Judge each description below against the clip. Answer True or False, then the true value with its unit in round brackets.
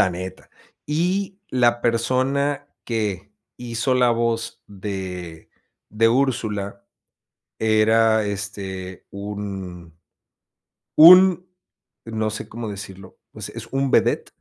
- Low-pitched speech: True (110 Hz)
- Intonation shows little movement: False (4.4 semitones)